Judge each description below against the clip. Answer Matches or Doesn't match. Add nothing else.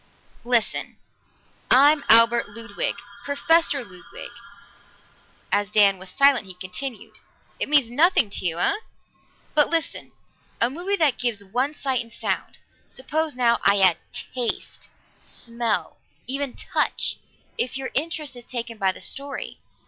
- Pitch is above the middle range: Matches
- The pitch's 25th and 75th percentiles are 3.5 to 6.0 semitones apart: Matches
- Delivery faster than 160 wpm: Doesn't match